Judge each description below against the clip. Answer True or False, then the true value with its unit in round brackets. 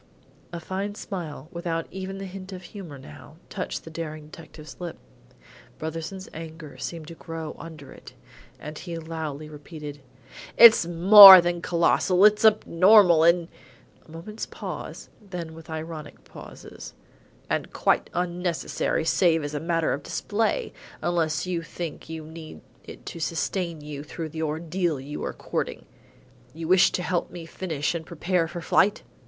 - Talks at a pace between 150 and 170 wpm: True (155 wpm)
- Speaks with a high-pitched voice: False (165 Hz)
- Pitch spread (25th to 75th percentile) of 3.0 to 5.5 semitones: False (2.4 semitones)